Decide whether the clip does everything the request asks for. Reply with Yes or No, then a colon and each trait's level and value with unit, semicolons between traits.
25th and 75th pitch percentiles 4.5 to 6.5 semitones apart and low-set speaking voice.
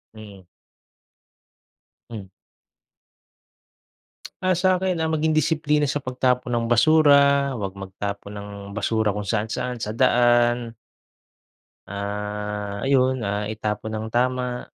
Yes: average, 5.0 semitones; low, 120 Hz